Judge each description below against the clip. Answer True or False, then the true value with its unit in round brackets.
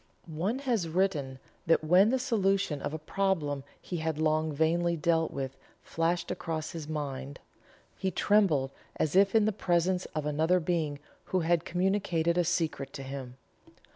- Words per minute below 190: True (160 wpm)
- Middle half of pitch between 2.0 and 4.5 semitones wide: True (3.6 semitones)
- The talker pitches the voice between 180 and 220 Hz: False (165 Hz)